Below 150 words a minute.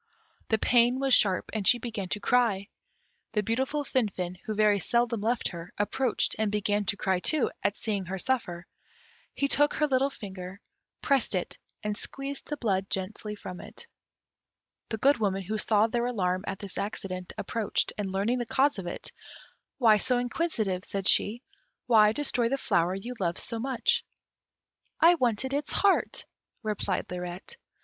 No: average, 165 wpm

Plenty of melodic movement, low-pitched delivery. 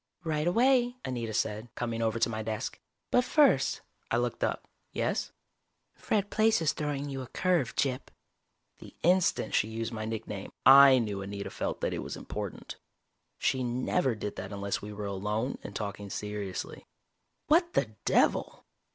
Yes: wide, 6.5 semitones; low, 115 Hz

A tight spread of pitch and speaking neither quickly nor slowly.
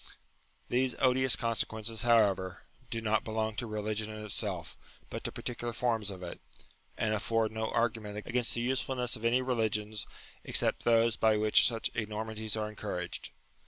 Yes: narrow, 1.7 semitones; average, 160 wpm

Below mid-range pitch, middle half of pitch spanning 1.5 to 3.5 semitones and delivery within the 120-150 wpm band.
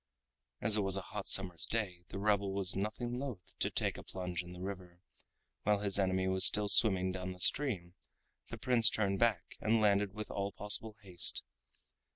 No: low, 100 Hz; narrow, 2.4 semitones; average, 190 wpm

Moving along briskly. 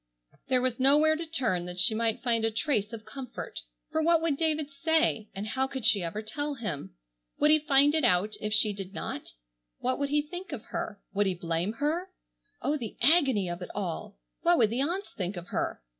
Yes: fast, 215 wpm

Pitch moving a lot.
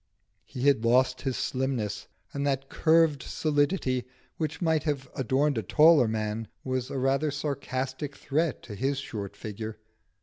No: average, 3.2 semitones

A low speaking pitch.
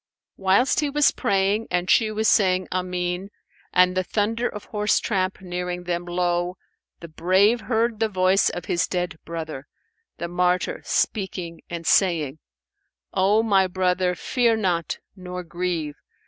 No: medium, 185 Hz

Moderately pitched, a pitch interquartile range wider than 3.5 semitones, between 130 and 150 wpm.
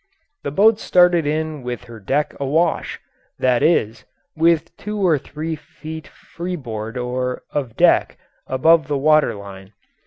Yes: medium, 150 Hz; average, 4.9 semitones; slow, 135 wpm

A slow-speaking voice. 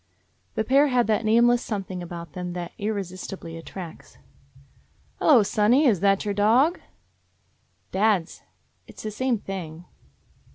Yes: slow, 130 wpm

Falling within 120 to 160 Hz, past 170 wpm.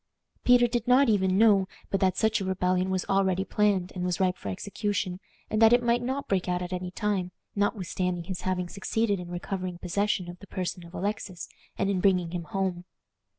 No: high, 190 Hz; average, 200 wpm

